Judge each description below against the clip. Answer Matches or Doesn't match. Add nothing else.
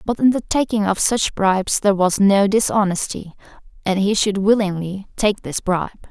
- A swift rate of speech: Doesn't match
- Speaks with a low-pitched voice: Doesn't match